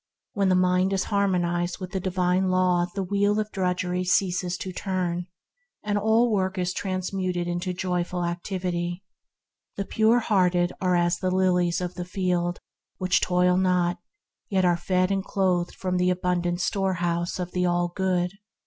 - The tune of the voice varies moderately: No, narrow, 1.2 semitones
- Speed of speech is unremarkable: Yes, average, 160 wpm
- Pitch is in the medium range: Yes, medium, 180 Hz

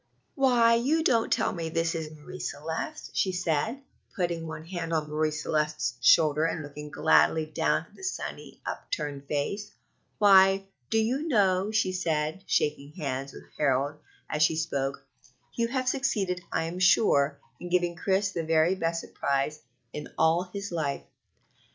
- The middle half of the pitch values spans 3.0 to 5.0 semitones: Yes, average, 4.5 semitones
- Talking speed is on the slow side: No, average, 155 wpm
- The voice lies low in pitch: No, medium, 165 Hz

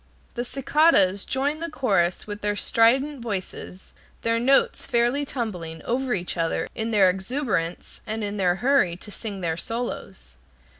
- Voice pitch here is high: Yes, high, 220 Hz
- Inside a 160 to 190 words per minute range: No, average, 150 wpm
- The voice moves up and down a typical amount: No, wide, 5.8 semitones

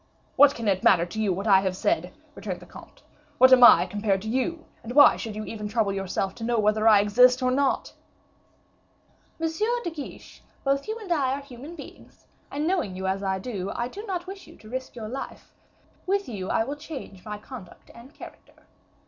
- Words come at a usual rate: No, fast, 210 wpm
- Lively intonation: Yes, wide, 5.7 semitones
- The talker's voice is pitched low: No, high, 240 Hz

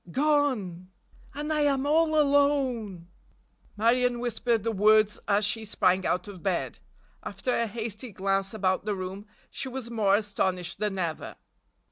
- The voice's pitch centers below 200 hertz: No, high, 215 Hz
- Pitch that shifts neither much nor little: Yes, average, 4.7 semitones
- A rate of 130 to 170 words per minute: Yes, average, 145 wpm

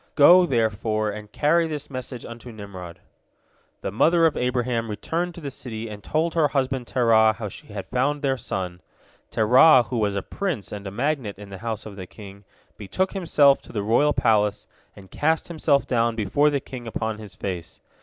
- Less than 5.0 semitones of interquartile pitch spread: No, wide, 5.6 semitones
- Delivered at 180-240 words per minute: Yes, average, 190 wpm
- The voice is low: Yes, low, 115 Hz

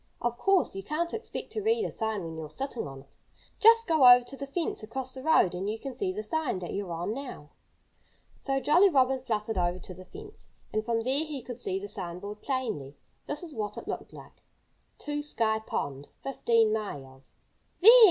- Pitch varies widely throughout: Yes, wide, 7.2 semitones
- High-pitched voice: Yes, high, 240 Hz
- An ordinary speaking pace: No, fast, 210 wpm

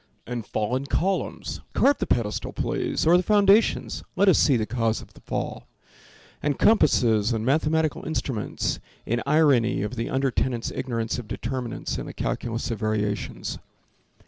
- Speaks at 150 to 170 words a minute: Yes, average, 155 wpm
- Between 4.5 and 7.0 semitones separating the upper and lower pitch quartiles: Yes, average, 5.2 semitones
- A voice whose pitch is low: Yes, low, 125 Hz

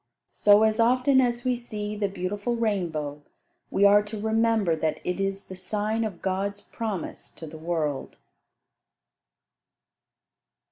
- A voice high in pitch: Yes, high, 205 Hz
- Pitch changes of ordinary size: Yes, average, 3.5 semitones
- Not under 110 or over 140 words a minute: Yes, slow, 135 wpm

